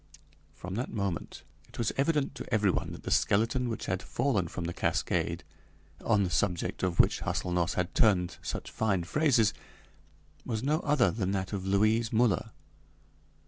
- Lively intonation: No, average, 4.3 semitones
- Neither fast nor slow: Yes, average, 160 wpm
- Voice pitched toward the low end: Yes, low, 105 Hz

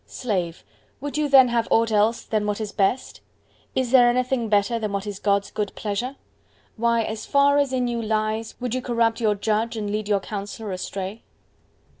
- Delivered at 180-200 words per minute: Yes, average, 190 wpm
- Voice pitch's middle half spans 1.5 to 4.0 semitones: Yes, average, 2.8 semitones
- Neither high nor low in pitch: No, high, 225 Hz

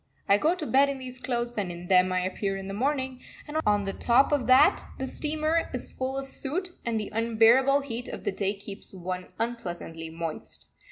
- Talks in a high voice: Yes, high, 235 Hz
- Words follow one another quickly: Yes, fast, 210 wpm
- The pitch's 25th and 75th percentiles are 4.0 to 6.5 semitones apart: Yes, wide, 5.6 semitones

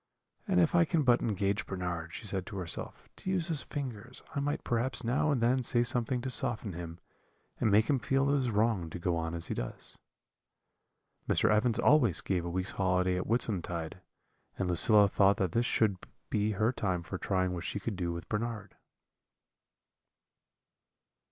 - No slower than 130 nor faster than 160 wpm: No, average, 185 wpm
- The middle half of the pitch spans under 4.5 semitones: No, average, 5.1 semitones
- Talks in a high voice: No, low, 105 Hz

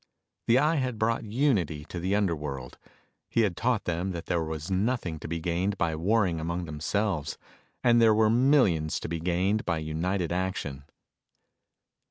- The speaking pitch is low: Yes, very low, 90 Hz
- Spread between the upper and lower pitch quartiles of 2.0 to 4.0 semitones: No, average, 5.2 semitones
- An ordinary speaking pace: Yes, average, 165 wpm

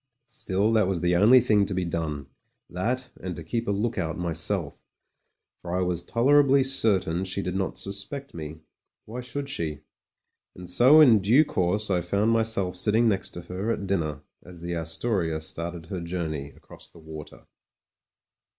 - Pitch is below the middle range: Yes, very low, 95 Hz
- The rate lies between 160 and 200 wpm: Yes, average, 170 wpm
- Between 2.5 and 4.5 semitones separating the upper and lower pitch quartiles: No, average, 4.9 semitones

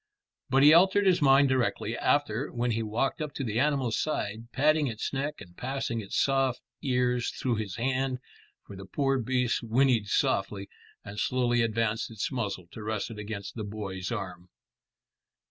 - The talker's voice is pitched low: Yes, low, 120 Hz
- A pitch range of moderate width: Yes, average, 4.1 semitones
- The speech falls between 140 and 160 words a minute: No, average, 170 wpm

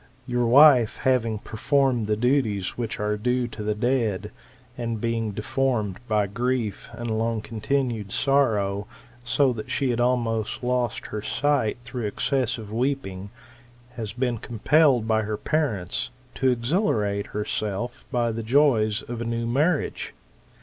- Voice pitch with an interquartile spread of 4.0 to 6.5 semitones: No, average, 3.0 semitones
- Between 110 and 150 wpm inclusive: Yes, average, 140 wpm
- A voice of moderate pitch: No, low, 115 Hz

